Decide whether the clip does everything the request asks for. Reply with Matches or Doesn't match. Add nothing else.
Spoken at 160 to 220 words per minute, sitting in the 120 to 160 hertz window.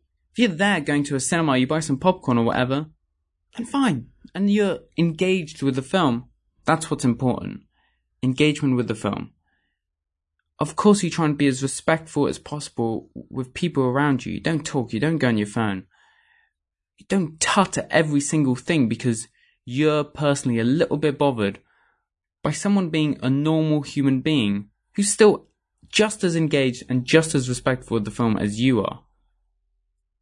Matches